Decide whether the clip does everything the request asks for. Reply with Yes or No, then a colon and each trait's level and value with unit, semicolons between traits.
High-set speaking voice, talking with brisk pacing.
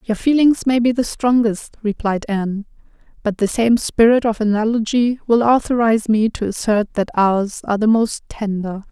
No: high, 220 Hz; average, 170 wpm